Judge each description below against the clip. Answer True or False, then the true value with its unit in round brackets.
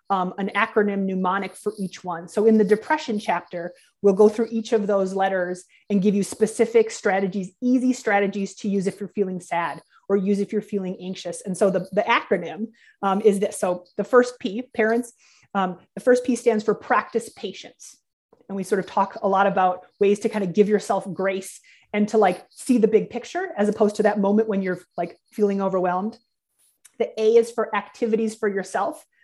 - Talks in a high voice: True (205 Hz)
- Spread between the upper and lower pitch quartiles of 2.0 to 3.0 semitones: True (2.5 semitones)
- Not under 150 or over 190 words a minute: False (200 wpm)